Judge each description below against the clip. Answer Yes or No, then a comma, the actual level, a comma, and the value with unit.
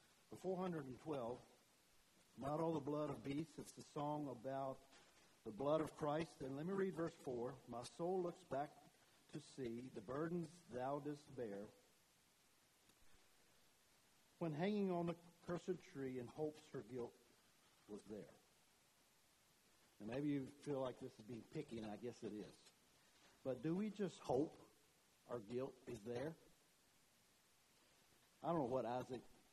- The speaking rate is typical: Yes, average, 155 wpm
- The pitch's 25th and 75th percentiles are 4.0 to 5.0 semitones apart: Yes, average, 4.5 semitones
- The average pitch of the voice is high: No, medium, 140 Hz